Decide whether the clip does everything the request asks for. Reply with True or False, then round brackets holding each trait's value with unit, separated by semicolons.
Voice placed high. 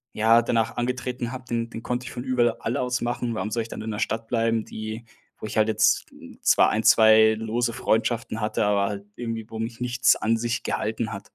False (115 Hz)